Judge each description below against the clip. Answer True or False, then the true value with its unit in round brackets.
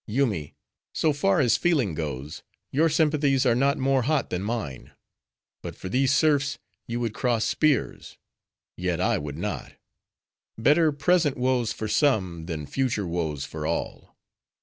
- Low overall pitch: True (125 Hz)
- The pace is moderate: True (150 wpm)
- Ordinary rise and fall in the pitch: False (8.1 semitones)